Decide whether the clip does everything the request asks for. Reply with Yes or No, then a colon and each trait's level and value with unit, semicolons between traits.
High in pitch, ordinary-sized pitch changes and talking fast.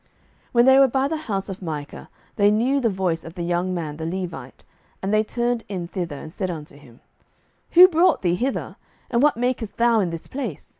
No: high, 195 Hz; wide, 6.3 semitones; fast, 215 wpm